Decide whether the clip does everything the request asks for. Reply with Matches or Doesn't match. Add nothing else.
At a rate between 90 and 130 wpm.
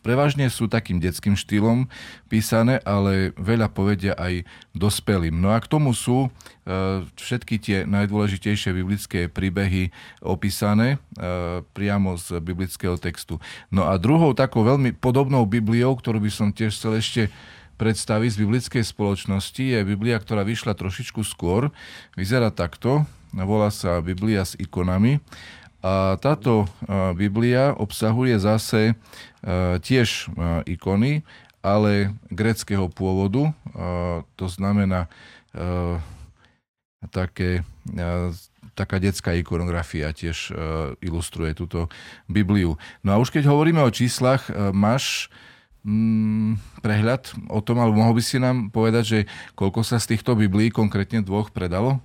Matches